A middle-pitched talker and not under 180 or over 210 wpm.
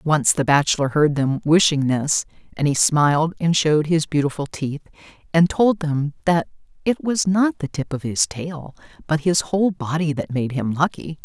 Yes: medium, 155 Hz; average, 185 wpm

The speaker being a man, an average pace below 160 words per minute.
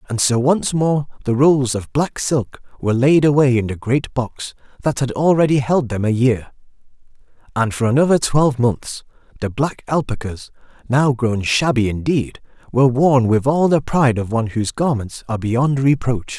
No: male; average, 175 wpm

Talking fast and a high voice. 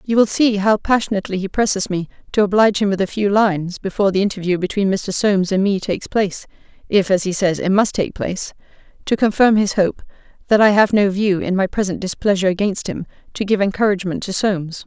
Yes: fast, 215 wpm; high, 195 Hz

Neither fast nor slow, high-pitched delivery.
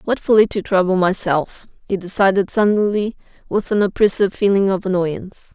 Yes: average, 150 wpm; high, 195 Hz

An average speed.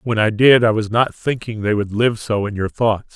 No: fast, 265 wpm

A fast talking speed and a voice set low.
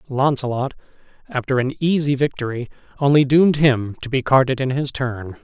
No: average, 155 wpm; low, 130 Hz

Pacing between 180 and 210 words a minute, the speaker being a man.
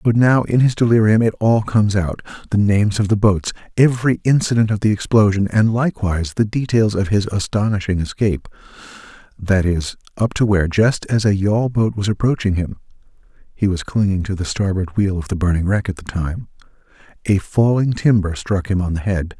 Yes: average, 190 wpm; male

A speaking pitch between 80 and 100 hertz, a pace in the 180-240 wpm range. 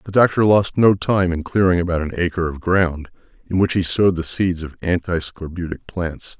Yes: very low, 90 Hz; fast, 205 wpm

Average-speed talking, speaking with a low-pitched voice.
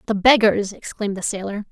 No: average, 175 wpm; high, 205 Hz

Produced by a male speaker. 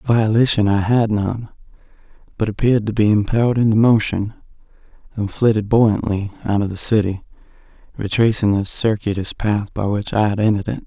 Yes: male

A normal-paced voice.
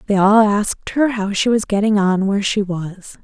No: fast, 220 wpm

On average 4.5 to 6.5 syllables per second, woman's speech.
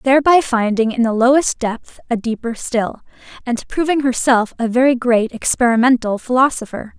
Yes: 5.0 syllables/s; female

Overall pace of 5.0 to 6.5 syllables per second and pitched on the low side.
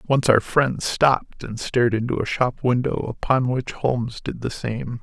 No: 4.6 syllables/s; low, 120 Hz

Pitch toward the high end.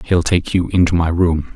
No: very low, 85 Hz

